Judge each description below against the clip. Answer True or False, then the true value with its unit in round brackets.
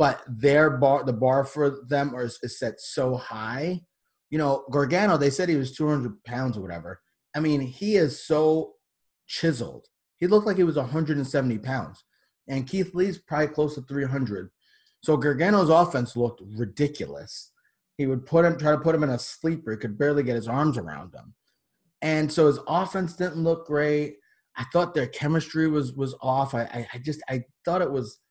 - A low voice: False (145 Hz)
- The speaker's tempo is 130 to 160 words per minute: False (190 wpm)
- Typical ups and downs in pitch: True (3.7 semitones)